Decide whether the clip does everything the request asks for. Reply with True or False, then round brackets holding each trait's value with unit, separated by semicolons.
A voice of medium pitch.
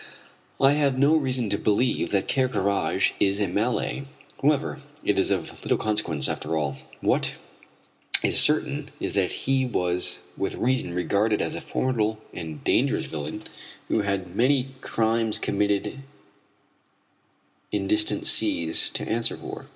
False (105 Hz)